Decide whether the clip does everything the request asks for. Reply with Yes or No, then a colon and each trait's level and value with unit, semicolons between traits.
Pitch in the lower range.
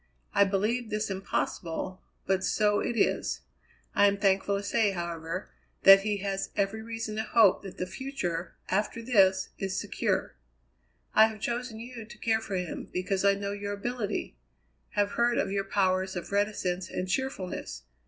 No: high, 200 Hz